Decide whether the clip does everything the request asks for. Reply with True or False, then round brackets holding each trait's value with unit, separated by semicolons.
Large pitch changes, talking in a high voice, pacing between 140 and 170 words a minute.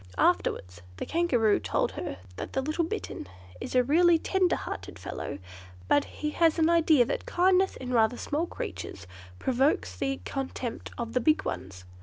True (6.1 semitones; 280 Hz; 165 wpm)